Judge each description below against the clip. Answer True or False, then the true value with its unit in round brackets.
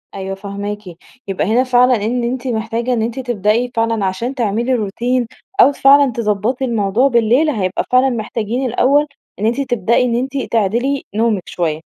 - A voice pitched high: True (235 Hz)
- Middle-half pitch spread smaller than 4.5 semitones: True (3.2 semitones)